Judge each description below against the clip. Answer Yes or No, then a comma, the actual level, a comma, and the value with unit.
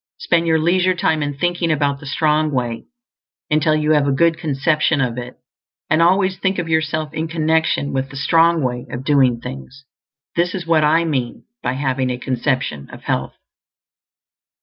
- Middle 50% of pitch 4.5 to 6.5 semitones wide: No, average, 3.5 semitones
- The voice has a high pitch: No, medium, 150 Hz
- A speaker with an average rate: Yes, average, 175 wpm